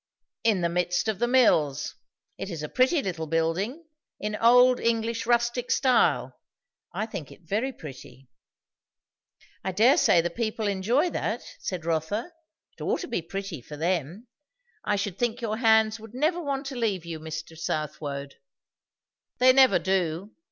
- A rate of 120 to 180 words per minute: Yes, average, 160 wpm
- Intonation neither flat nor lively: No, wide, 6.4 semitones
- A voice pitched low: No, high, 210 Hz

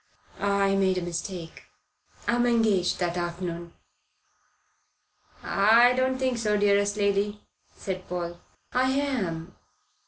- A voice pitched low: No, high, 200 Hz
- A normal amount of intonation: Yes, average, 4.6 semitones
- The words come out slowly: Yes, slow, 105 wpm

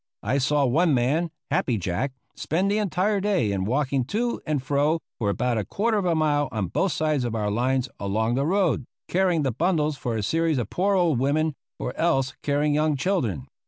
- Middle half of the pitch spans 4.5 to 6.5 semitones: Yes, wide, 5.6 semitones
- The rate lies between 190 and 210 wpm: Yes, average, 200 wpm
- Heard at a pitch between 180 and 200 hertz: No, medium, 145 Hz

